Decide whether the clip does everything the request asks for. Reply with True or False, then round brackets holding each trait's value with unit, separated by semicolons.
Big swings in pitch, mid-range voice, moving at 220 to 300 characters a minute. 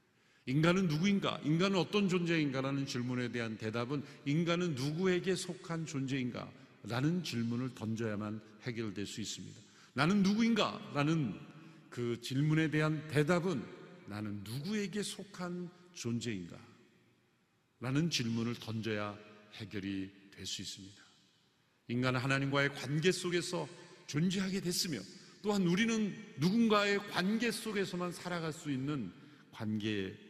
True (7.2 semitones; 150 Hz; 290 characters per minute)